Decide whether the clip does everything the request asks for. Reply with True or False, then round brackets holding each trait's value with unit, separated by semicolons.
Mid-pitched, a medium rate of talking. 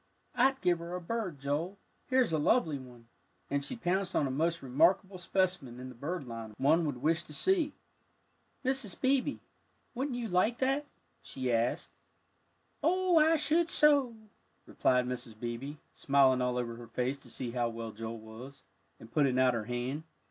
True (150 Hz; 170 wpm)